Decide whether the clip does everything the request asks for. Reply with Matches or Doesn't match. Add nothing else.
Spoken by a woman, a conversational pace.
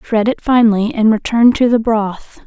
Matches